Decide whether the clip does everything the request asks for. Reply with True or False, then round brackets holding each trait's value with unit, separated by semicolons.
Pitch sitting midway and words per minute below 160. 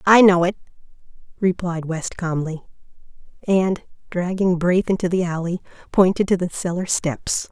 True (180 Hz; 135 wpm)